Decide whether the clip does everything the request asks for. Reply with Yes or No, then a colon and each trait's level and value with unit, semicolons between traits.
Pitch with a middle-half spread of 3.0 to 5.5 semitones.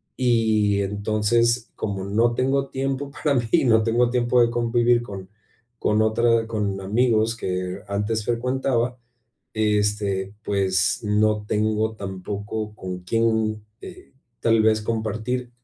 No: narrow, 2.4 semitones